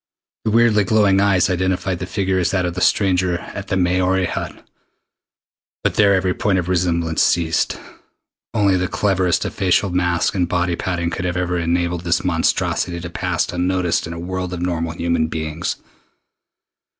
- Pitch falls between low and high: No, very low, 90 Hz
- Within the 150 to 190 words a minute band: Yes, average, 170 wpm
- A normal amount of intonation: No, narrow, 1.6 semitones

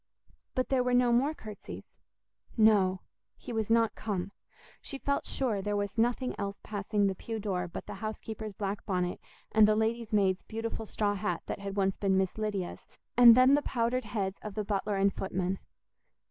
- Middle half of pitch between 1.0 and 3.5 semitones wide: Yes, average, 2.8 semitones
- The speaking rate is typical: Yes, average, 185 wpm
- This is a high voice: Yes, high, 210 Hz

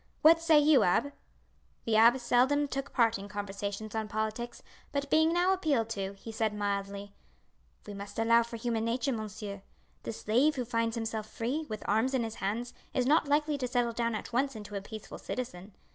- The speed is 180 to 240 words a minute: Yes, average, 190 wpm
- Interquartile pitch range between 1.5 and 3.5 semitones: No, average, 4.0 semitones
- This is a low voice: No, high, 230 Hz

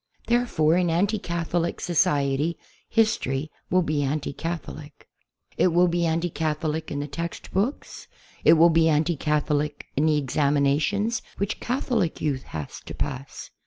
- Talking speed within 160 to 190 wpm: No, average, 145 wpm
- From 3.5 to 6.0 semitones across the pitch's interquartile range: No, average, 3.1 semitones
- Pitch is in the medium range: Yes, medium, 160 Hz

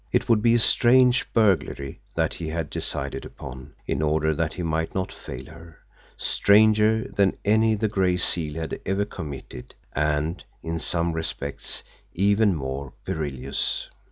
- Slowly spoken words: No, average, 150 wpm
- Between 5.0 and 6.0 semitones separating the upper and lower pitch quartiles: Yes, average, 5.3 semitones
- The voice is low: Yes, very low, 85 Hz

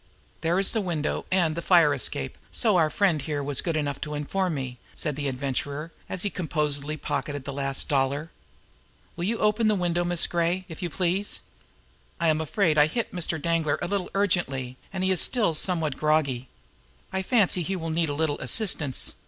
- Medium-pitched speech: Yes, medium, 165 Hz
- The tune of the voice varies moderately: Yes, average, 4.1 semitones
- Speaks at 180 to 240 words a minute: Yes, average, 195 wpm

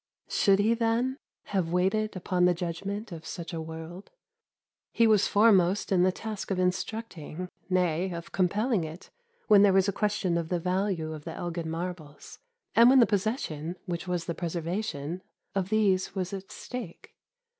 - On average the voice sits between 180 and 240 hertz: Yes, medium, 185 Hz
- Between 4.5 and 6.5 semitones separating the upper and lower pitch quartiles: No, average, 3.4 semitones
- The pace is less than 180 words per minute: Yes, average, 165 wpm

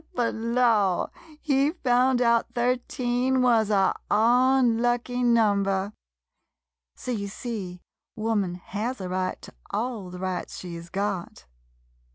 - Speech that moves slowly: Yes, slow, 130 wpm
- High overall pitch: Yes, high, 230 Hz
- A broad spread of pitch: No, average, 3.9 semitones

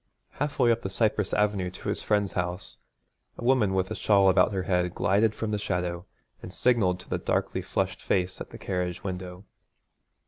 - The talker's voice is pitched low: Yes, very low, 95 Hz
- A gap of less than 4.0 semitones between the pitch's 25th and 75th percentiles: Yes, average, 2.7 semitones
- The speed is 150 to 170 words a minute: No, average, 195 wpm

